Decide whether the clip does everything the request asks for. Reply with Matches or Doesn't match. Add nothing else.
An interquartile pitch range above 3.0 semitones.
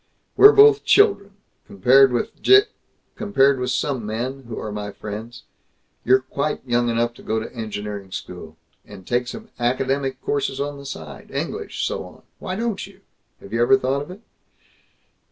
Matches